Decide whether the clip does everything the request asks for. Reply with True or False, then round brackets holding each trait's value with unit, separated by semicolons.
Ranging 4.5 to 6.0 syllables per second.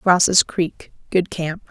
False (2.9 syllables/s)